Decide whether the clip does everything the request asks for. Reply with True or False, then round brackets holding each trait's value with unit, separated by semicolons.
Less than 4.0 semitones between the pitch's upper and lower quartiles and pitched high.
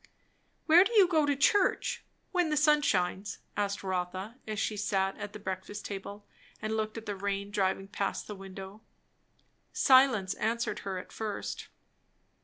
False (4.8 semitones; 205 Hz)